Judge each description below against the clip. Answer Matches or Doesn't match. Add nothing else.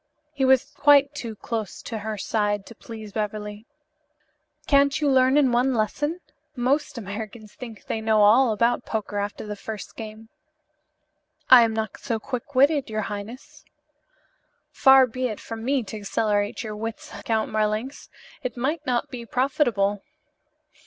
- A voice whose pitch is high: Matches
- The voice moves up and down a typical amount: Matches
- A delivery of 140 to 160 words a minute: Matches